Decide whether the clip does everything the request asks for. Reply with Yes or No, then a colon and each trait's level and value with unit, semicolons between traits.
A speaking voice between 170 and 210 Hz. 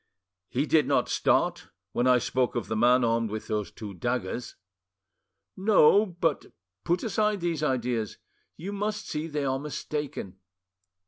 No: low, 135 Hz